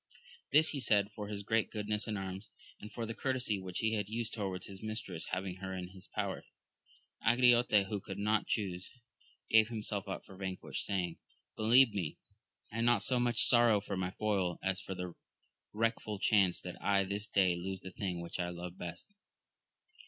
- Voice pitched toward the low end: Yes, low, 100 Hz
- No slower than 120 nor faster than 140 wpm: No, average, 185 wpm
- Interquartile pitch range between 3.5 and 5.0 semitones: No, average, 3.0 semitones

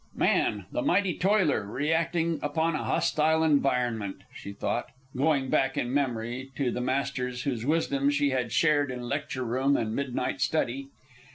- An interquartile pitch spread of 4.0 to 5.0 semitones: No, average, 3.6 semitones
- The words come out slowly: No, average, 155 wpm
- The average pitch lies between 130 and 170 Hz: Yes, low, 135 Hz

